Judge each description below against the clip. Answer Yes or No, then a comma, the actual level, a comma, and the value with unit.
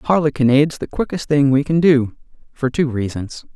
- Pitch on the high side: No, medium, 140 Hz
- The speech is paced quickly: No, average, 185 wpm